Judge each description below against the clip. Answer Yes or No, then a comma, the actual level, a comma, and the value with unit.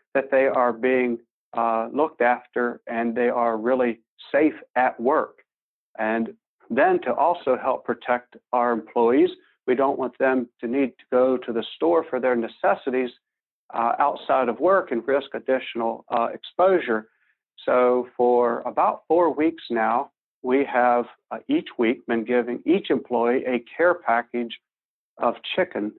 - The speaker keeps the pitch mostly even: Yes, narrow, 2.2 semitones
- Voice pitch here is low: Yes, low, 125 Hz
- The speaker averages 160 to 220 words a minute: No, average, 150 wpm